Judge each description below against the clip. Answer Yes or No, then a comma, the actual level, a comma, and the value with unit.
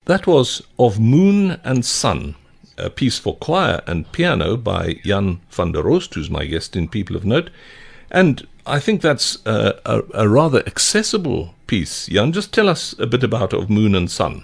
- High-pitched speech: No, low, 120 Hz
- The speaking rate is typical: Yes, average, 185 wpm